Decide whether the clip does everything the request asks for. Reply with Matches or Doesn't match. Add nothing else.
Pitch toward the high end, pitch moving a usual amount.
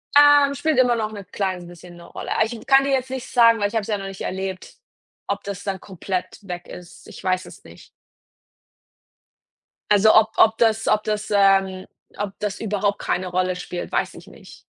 Matches